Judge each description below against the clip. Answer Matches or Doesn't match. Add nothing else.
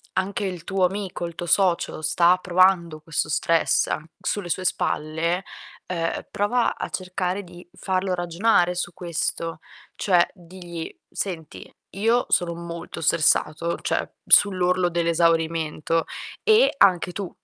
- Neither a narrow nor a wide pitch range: Doesn't match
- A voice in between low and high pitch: Matches